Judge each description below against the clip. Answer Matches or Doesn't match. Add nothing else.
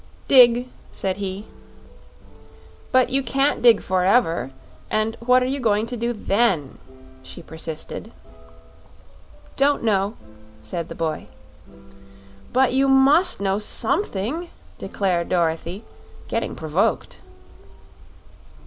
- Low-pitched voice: Doesn't match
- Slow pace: Matches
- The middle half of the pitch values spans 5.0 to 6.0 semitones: Matches